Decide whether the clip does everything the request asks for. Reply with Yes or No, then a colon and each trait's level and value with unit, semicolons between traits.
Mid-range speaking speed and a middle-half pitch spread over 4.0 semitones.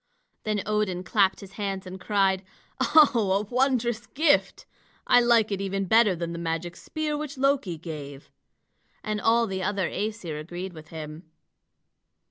Yes: average, 145 wpm; average, 4.8 semitones